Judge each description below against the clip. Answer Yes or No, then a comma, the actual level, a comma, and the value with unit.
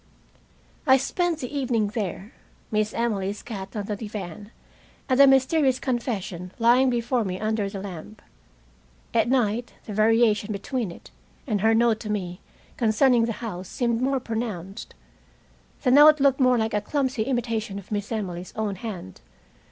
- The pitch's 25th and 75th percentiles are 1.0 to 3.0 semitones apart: No, average, 3.5 semitones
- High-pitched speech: Yes, high, 225 Hz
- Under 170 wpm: Yes, average, 155 wpm